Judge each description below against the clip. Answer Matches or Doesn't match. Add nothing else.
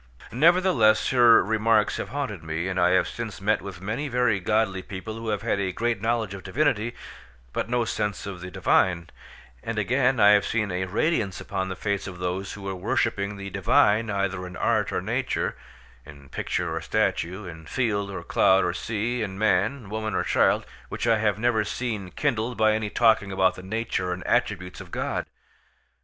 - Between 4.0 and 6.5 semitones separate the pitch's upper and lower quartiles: Doesn't match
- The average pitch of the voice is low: Matches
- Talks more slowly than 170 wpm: Doesn't match